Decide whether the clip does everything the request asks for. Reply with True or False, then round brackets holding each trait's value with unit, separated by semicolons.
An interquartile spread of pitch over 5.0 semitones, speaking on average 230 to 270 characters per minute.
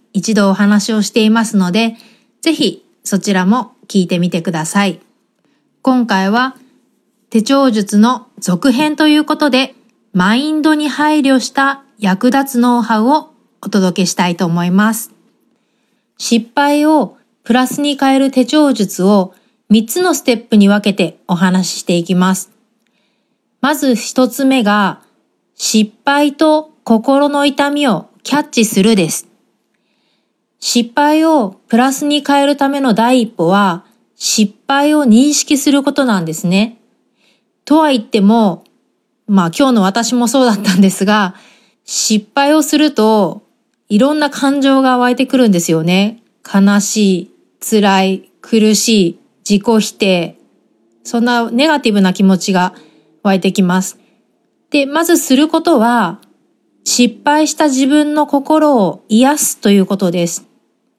True (5.6 semitones; 255 characters per minute)